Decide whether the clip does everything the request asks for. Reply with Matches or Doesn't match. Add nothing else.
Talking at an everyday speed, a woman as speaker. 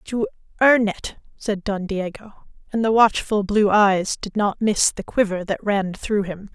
Matches